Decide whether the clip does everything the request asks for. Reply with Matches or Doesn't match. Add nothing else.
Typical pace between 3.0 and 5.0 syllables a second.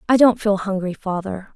Doesn't match